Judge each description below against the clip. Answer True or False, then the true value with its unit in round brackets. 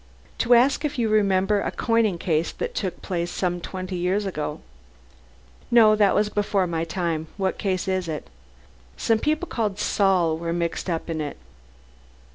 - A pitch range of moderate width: True (3.9 semitones)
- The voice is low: False (190 Hz)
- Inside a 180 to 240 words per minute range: False (165 wpm)